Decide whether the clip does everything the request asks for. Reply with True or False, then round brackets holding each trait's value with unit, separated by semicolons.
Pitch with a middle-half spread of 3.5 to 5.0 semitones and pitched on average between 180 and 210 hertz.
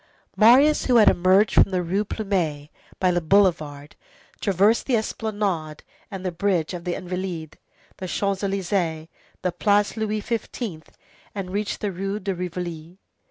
False (3.1 semitones; 190 Hz)